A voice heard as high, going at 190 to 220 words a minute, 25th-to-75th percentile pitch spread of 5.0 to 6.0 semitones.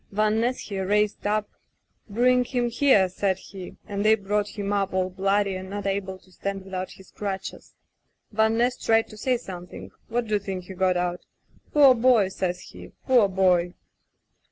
No: high, 200 Hz; average, 195 wpm; average, 2.7 semitones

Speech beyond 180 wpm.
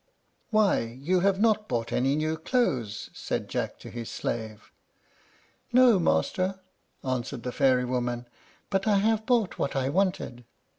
No: average, 145 wpm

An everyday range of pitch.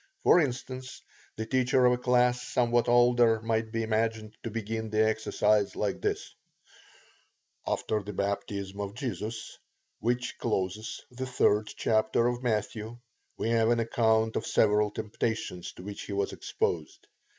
No: narrow, 2.2 semitones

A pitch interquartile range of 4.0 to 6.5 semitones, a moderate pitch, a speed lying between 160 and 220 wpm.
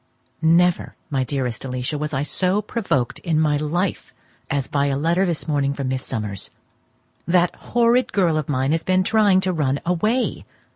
Yes: average, 5.1 semitones; medium, 155 Hz; average, 175 wpm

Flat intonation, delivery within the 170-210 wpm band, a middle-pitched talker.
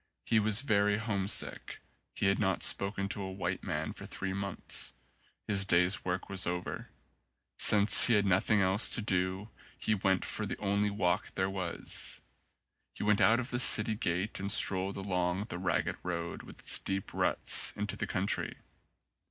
No: narrow, 1.8 semitones; average, 175 wpm; low, 100 Hz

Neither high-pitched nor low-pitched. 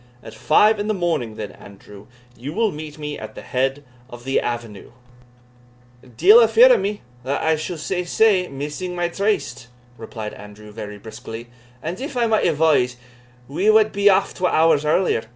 Yes: medium, 155 Hz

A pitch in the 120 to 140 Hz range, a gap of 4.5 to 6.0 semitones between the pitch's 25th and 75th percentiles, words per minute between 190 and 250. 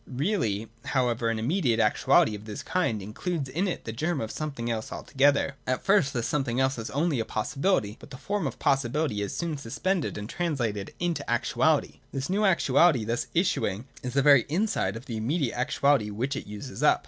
Yes: low, 135 Hz; wide, 5.5 semitones; average, 195 wpm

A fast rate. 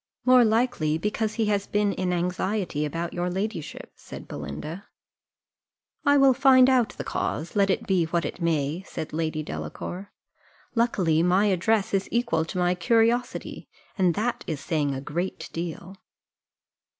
No: average, 150 wpm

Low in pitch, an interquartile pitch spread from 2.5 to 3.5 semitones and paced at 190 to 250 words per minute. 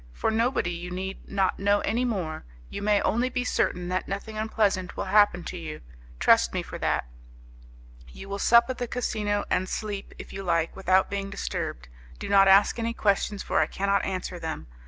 No: high, 195 Hz; average, 2.9 semitones; average, 195 wpm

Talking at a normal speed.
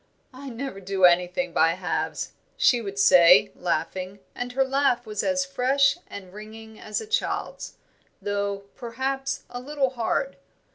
Yes: average, 145 wpm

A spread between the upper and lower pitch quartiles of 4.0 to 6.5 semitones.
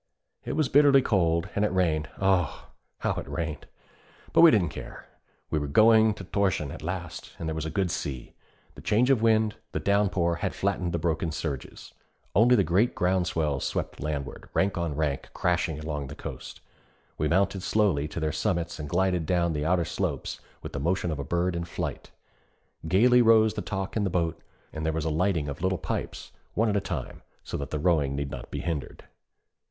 Yes: average, 4.3 semitones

